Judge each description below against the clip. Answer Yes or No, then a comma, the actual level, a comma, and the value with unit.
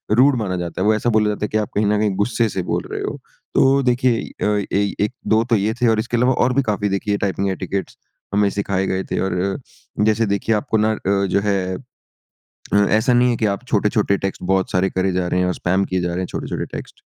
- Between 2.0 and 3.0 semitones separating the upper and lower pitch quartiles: Yes, average, 2.7 semitones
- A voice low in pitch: Yes, low, 105 Hz